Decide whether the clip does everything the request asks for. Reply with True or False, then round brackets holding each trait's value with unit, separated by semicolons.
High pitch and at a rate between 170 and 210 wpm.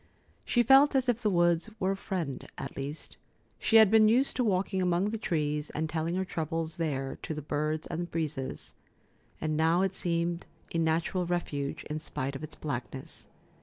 False (170 Hz; 185 wpm)